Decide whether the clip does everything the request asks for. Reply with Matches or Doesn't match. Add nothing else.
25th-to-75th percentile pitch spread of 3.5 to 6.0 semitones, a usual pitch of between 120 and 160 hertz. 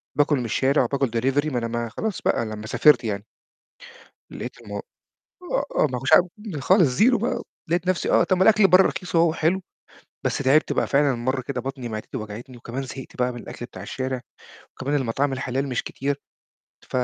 Matches